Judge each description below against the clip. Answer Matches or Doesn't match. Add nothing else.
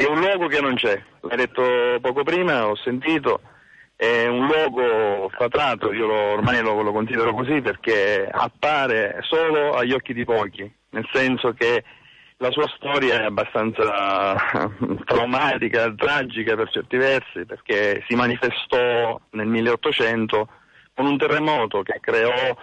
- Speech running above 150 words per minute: Doesn't match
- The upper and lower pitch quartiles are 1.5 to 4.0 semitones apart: Doesn't match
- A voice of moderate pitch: Doesn't match